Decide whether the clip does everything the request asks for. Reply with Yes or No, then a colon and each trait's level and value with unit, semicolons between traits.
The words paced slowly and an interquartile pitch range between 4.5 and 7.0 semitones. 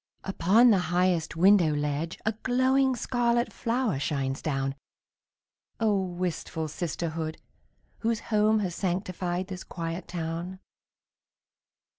Yes: slow, 105 wpm; average, 4.8 semitones